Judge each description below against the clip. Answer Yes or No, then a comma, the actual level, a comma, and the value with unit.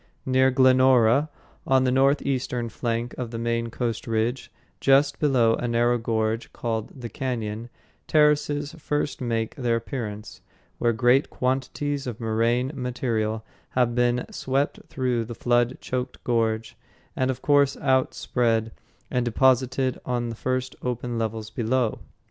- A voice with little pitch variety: Yes, narrow, 2.2 semitones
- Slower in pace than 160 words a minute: Yes, slow, 135 wpm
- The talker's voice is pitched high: No, low, 125 Hz